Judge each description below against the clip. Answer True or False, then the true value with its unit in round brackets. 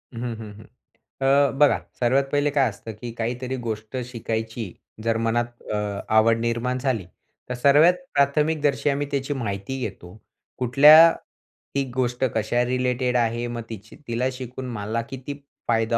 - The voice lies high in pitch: False (120 Hz)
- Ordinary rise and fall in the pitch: True (3.0 semitones)